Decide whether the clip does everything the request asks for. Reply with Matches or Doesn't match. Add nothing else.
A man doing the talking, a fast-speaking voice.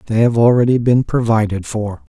Doesn't match